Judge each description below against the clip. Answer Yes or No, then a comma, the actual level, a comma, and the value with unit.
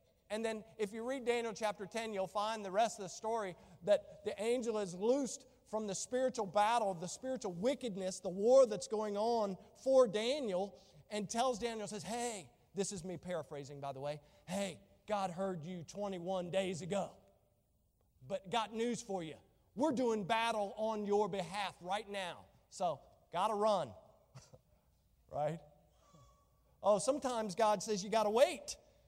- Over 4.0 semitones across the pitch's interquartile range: No, average, 3.2 semitones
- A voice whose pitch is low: No, high, 210 Hz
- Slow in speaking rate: No, average, 165 wpm